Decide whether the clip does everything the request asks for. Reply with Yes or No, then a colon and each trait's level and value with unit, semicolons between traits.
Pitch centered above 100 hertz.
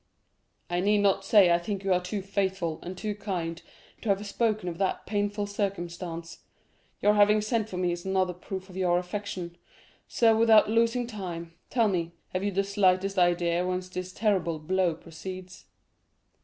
Yes: high, 190 Hz